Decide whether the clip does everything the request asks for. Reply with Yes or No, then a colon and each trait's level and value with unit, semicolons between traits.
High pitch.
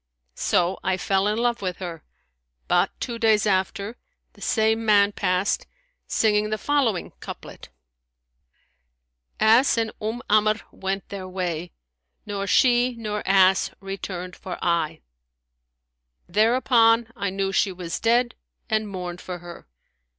Yes: high, 200 Hz